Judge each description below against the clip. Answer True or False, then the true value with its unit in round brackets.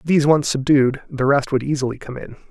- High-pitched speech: False (140 Hz)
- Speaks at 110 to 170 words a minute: False (215 wpm)